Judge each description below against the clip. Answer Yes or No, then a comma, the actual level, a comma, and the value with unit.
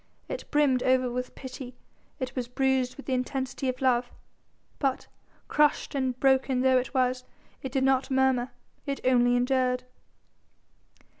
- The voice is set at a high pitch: Yes, very high, 260 Hz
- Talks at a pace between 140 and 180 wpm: Yes, average, 145 wpm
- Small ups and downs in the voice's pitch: Yes, narrow, 1.0 semitones